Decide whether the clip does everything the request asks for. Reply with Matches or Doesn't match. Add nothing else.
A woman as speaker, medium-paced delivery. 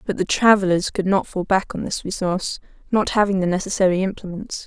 Matches